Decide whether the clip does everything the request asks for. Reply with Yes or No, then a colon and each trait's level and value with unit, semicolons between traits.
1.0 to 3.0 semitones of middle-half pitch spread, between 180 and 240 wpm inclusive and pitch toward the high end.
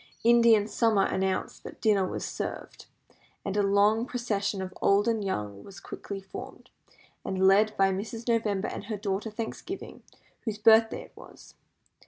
No: narrow, 2.5 semitones; average, 155 wpm; high, 205 Hz